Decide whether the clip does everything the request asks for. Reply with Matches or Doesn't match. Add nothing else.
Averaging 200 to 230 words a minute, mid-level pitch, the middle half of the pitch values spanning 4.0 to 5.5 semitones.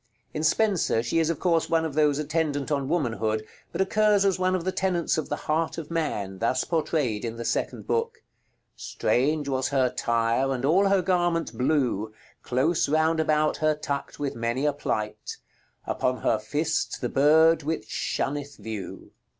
Doesn't match